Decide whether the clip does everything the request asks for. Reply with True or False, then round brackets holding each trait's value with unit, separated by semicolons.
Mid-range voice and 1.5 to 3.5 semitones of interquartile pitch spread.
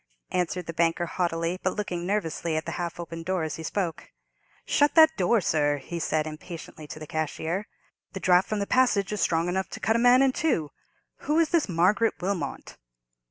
False (180 Hz; 4.2 semitones)